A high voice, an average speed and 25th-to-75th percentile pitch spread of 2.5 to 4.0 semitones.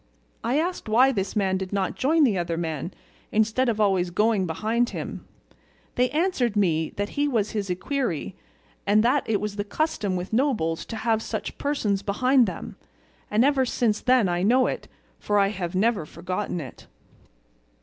No: high, 210 Hz; average, 175 wpm; average, 5.1 semitones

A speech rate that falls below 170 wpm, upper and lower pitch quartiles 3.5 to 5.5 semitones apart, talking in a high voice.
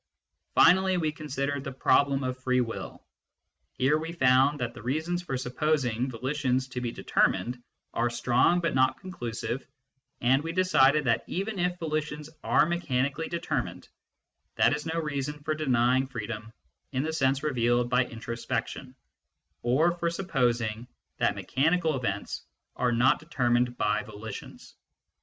No: average, 145 wpm; average, 4.3 semitones; low, 130 Hz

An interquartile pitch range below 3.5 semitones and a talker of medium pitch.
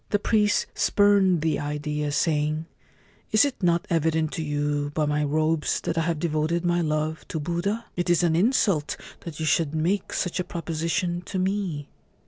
Yes: average, 2.8 semitones; medium, 165 Hz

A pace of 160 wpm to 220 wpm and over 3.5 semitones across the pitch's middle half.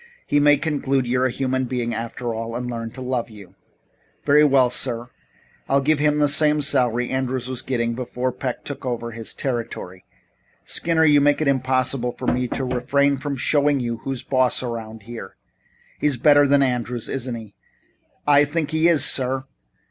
No: average, 180 wpm; average, 3.0 semitones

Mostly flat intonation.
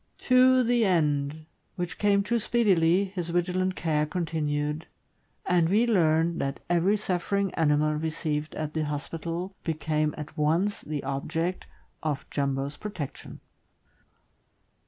No: average, 3.7 semitones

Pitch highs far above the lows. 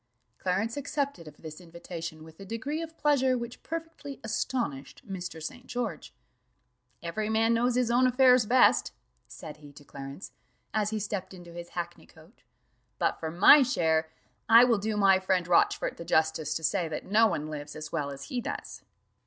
Yes: wide, 7.2 semitones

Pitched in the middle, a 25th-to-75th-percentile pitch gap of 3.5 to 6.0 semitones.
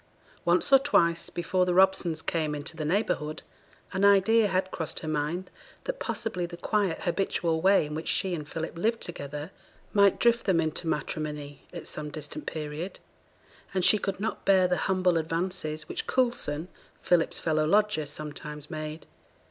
Yes: medium, 170 Hz; average, 3.8 semitones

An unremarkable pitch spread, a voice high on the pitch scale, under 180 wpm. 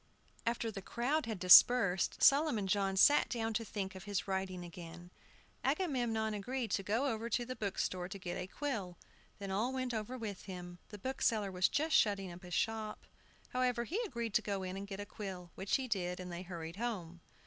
No: average, 4.3 semitones; high, 205 Hz; average, 200 wpm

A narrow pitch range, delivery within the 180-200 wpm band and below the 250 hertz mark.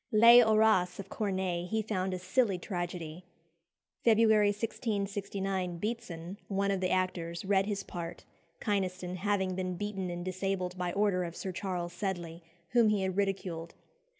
No: narrow, 2.3 semitones; average, 150 wpm; high, 190 Hz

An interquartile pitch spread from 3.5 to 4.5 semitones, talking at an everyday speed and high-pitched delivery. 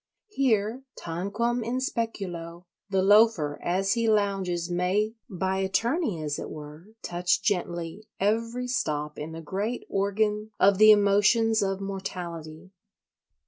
No: average, 4.0 semitones; slow, 125 wpm; high, 195 Hz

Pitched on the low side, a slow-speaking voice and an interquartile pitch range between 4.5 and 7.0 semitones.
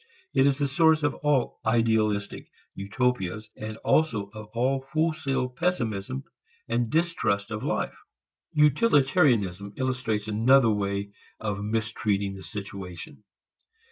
Yes: low, 115 Hz; slow, 110 wpm; average, 5.0 semitones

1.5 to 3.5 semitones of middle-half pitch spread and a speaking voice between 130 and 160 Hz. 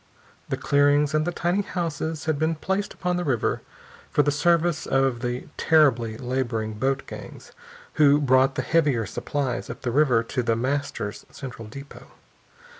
No: average, 4.1 semitones; medium, 140 Hz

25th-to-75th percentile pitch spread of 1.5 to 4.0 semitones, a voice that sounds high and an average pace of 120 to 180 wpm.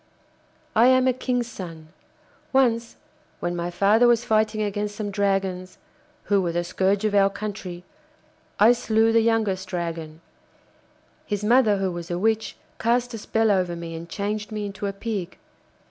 Yes: average, 3.4 semitones; high, 205 Hz; average, 160 wpm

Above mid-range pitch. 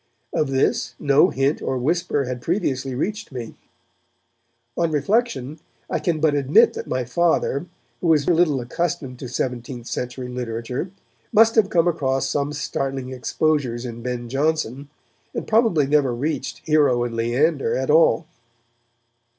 No: medium, 140 Hz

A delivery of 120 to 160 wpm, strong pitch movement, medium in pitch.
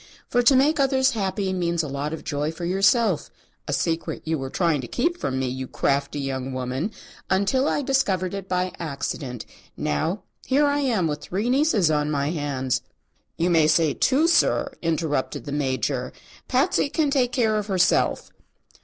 No: average, 180 wpm; wide, 8.8 semitones; medium, 170 Hz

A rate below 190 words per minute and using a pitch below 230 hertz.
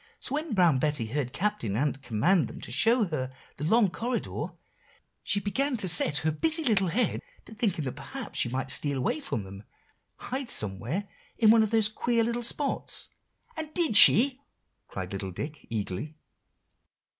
Yes: average, 175 wpm; medium, 185 Hz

